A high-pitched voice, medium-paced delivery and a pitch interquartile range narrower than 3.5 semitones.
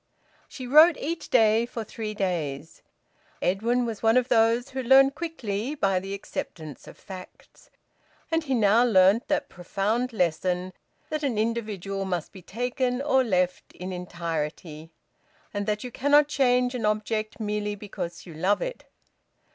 No: high, 215 Hz; average, 150 wpm; average, 5.0 semitones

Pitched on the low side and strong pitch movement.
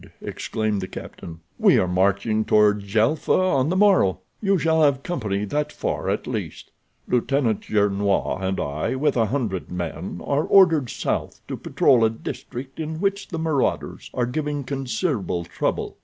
Yes: low, 125 Hz; wide, 7.0 semitones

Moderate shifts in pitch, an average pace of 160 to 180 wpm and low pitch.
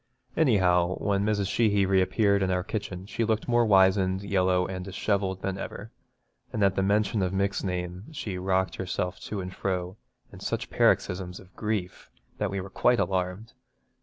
No: narrow, 1.9 semitones; average, 170 wpm; very low, 95 Hz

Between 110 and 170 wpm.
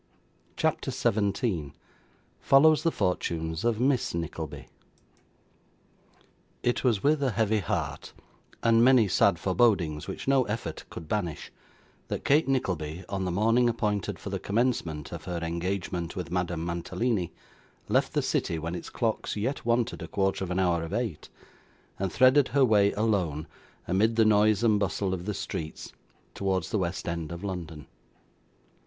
Yes: average, 150 wpm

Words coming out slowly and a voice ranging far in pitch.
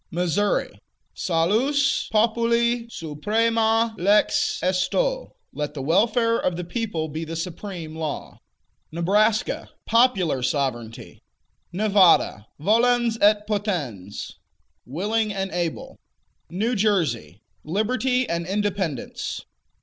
Yes: slow, 95 wpm; wide, 5.7 semitones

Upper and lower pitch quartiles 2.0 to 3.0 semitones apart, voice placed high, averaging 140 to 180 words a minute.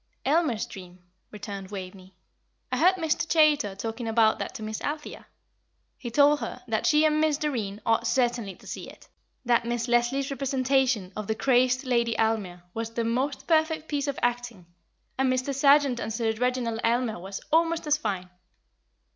No: average, 4.4 semitones; high, 240 Hz; average, 170 wpm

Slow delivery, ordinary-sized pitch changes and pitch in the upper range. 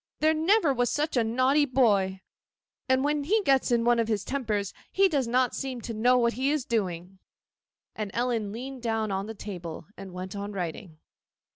No: average, 180 wpm; average, 4.9 semitones; high, 235 Hz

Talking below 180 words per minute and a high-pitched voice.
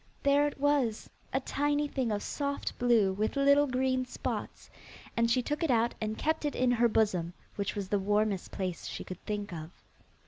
No: average, 195 wpm; high, 235 Hz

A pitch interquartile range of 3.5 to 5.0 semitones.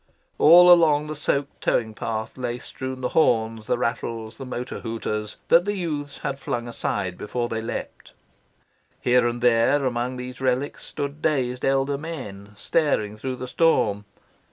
Yes: average, 4.0 semitones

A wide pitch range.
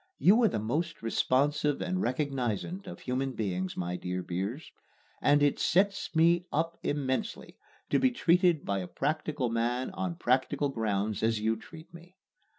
Yes: wide, 6.9 semitones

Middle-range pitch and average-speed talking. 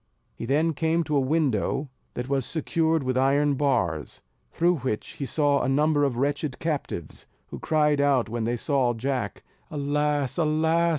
Yes: medium, 145 Hz; average, 165 wpm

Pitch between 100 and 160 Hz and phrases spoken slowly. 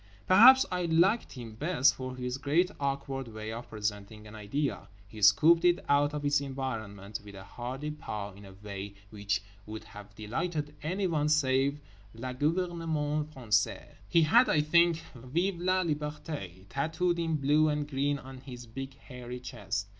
No: low, 135 Hz; average, 160 wpm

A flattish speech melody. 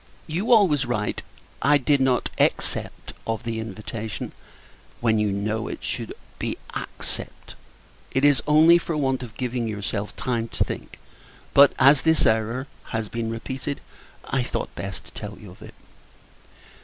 No: average, 4.3 semitones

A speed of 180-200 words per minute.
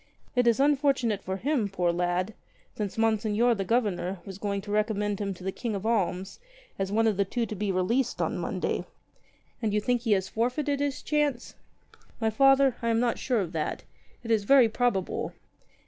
Yes: average, 195 wpm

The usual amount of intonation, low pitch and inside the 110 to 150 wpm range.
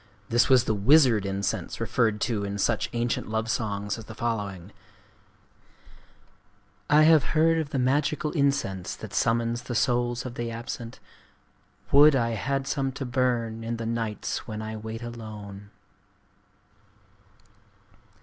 Yes: average, 3.3 semitones; low, 115 Hz; average, 140 wpm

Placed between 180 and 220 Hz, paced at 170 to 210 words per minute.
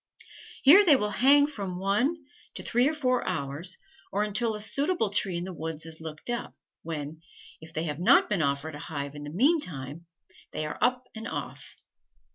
Yes: high, 190 Hz; average, 195 wpm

